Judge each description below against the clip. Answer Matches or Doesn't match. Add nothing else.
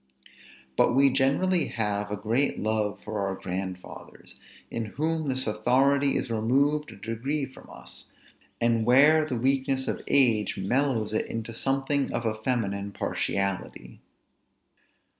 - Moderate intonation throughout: Matches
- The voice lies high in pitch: Doesn't match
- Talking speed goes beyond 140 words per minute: Doesn't match